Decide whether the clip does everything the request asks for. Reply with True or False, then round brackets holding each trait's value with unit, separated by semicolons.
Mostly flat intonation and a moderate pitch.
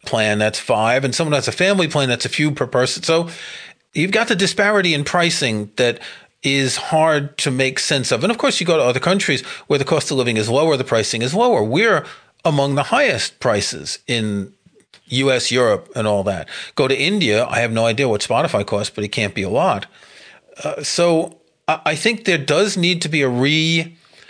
False (5.4 semitones; 145 Hz)